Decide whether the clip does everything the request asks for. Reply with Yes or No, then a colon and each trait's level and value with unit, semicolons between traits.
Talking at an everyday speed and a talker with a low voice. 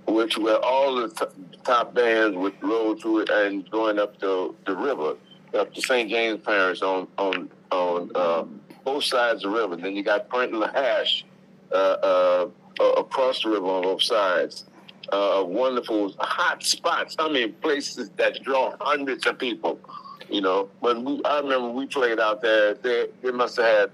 Yes: average, 180 wpm; low, 115 Hz